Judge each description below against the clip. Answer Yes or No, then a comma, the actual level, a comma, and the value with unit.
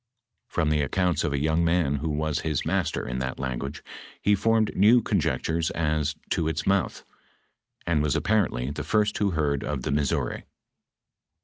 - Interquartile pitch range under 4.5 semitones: Yes, average, 4.1 semitones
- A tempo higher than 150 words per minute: Yes, average, 170 wpm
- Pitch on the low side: Yes, very low, 80 Hz